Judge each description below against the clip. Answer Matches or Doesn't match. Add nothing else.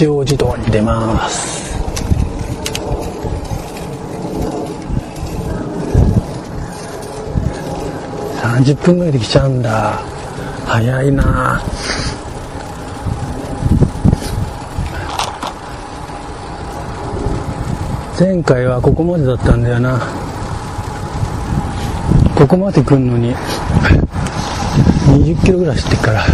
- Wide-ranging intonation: Doesn't match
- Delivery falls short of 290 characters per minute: Matches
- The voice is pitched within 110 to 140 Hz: Matches